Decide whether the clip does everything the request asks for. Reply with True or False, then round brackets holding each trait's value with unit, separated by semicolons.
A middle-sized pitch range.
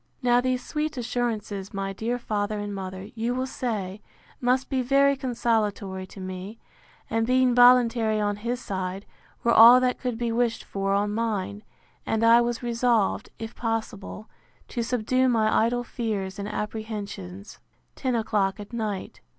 True (3.1 semitones)